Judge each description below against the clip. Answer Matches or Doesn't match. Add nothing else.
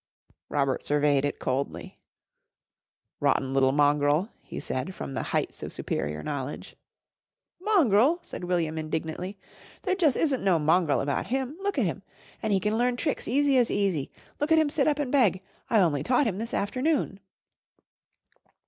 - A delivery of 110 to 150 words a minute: Doesn't match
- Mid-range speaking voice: Doesn't match